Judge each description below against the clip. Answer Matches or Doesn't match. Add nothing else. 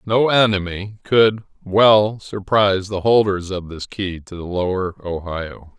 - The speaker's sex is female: Doesn't match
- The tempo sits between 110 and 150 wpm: Matches